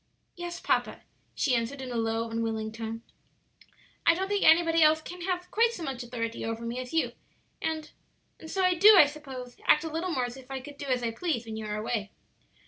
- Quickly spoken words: Yes, fast, 220 wpm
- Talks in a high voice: Yes, very high, 270 Hz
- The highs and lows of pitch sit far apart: Yes, wide, 6.4 semitones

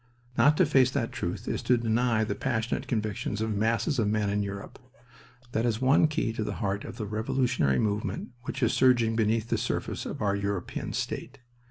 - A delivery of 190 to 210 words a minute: Yes, average, 195 wpm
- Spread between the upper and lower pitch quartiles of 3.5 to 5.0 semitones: No, average, 3.0 semitones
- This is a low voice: Yes, low, 110 Hz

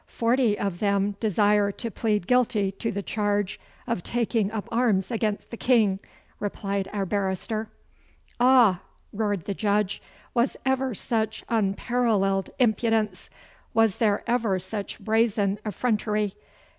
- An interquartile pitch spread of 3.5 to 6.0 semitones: No, narrow, 2.5 semitones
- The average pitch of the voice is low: No, high, 210 Hz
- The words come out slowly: Yes, slow, 125 wpm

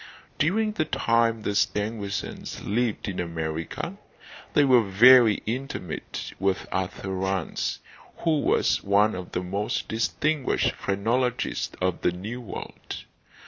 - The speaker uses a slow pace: Yes, slow, 120 wpm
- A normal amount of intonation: Yes, average, 4.5 semitones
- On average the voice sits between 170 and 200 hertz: No, low, 105 Hz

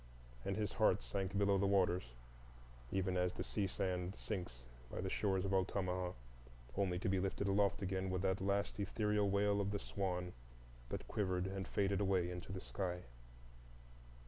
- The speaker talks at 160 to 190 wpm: Yes, average, 170 wpm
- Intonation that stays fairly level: Yes, narrow, 1.6 semitones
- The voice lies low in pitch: Yes, very low, 95 Hz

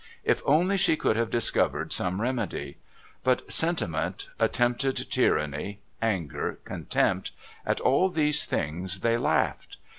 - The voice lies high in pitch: No, low, 120 Hz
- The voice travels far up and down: Yes, wide, 7.9 semitones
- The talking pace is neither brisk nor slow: No, slow, 120 wpm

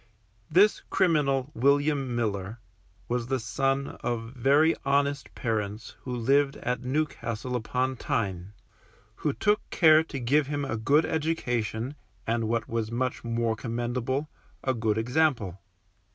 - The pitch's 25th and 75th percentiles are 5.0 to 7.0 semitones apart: No, average, 3.7 semitones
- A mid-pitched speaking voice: No, low, 125 Hz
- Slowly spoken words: Yes, slow, 130 wpm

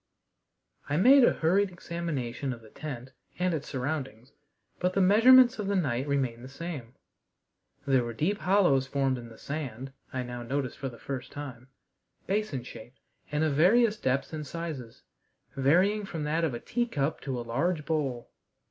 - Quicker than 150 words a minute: Yes, average, 170 wpm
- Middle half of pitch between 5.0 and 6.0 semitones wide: Yes, wide, 5.6 semitones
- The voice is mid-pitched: Yes, medium, 145 Hz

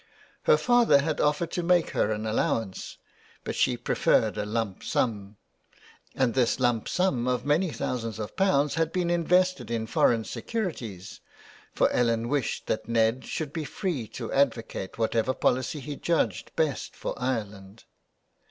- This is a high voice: No, low, 125 Hz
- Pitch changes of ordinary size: No, wide, 6.1 semitones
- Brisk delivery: No, average, 150 wpm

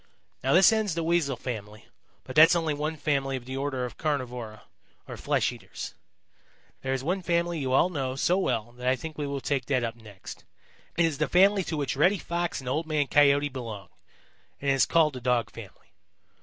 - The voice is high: No, medium, 140 Hz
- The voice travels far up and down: No, average, 4.3 semitones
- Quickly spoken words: Yes, fast, 210 wpm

